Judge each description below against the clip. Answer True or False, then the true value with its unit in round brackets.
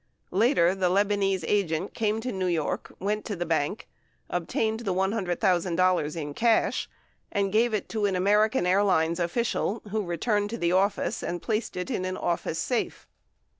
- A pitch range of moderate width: True (3.4 semitones)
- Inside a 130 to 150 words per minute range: False (165 wpm)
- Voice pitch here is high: True (195 Hz)